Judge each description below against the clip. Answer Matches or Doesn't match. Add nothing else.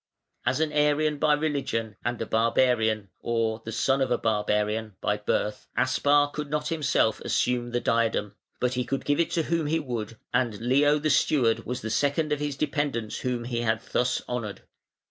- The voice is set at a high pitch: Doesn't match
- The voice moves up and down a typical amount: Matches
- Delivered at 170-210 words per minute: Matches